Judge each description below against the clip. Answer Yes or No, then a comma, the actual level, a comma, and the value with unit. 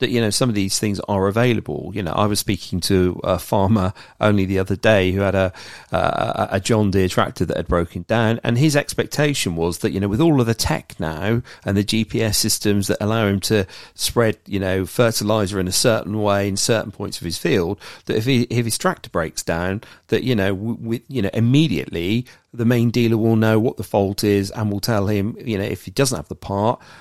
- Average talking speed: No, fast, 235 wpm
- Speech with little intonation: No, average, 3.2 semitones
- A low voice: Yes, low, 105 Hz